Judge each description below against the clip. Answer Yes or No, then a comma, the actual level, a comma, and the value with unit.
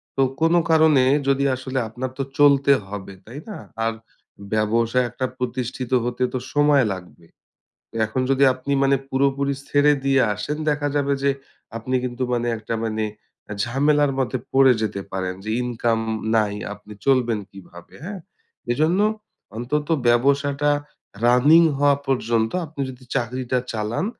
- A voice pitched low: Yes, low, 130 Hz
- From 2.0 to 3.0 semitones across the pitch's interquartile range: No, average, 3.5 semitones